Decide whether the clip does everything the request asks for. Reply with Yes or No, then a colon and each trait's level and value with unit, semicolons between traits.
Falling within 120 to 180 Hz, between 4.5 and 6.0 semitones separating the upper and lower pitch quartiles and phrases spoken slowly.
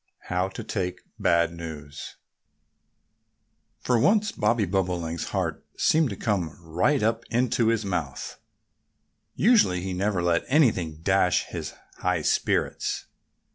No: very low, 95 Hz; average, 5.3 semitones; slow, 125 wpm